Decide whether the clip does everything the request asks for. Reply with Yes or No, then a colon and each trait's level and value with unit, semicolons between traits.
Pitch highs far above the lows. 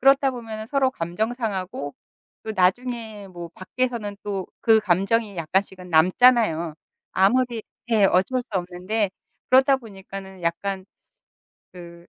No: average, 4.5 semitones